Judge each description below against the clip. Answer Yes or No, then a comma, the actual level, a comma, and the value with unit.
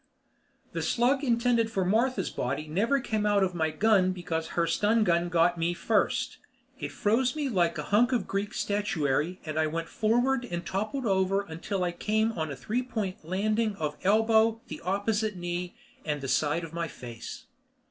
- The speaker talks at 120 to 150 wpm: No, average, 185 wpm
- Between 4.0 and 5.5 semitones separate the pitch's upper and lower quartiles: Yes, average, 4.8 semitones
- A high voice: Yes, high, 195 Hz